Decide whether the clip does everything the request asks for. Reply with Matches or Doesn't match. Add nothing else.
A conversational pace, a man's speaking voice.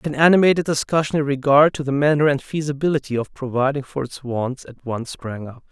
Doesn't match